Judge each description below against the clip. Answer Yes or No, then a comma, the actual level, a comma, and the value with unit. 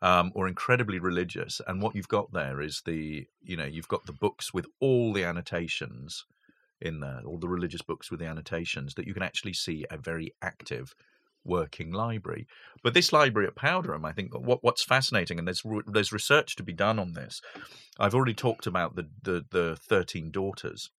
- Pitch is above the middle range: No, very low, 90 Hz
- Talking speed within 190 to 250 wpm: Yes, average, 195 wpm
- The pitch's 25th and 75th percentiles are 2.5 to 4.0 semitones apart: No, average, 4.8 semitones